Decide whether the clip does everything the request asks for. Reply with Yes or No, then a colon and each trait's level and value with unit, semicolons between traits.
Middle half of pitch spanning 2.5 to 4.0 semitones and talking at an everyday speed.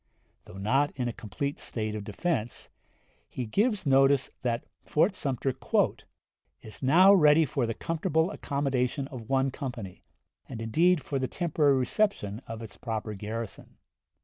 No: average, 4.9 semitones; average, 145 wpm